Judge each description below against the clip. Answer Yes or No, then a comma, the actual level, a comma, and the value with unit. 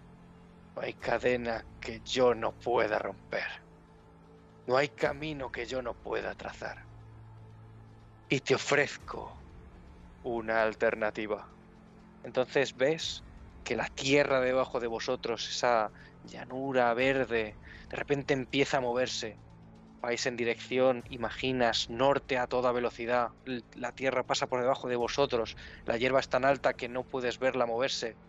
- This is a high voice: No, low, 125 Hz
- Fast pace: No, average, 130 wpm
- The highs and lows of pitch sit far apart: No, average, 2.8 semitones